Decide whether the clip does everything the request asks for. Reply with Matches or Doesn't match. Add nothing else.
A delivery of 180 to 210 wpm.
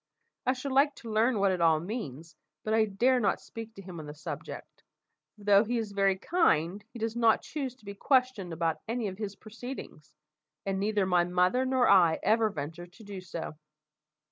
Matches